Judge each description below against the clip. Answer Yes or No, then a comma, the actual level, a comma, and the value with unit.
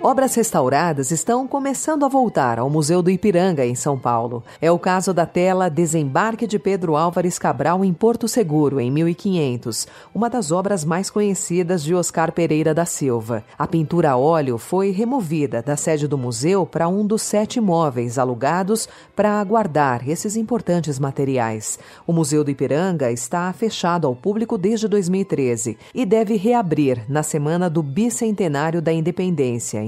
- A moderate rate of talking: Yes, average, 155 wpm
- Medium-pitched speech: Yes, medium, 170 Hz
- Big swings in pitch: Yes, wide, 5.8 semitones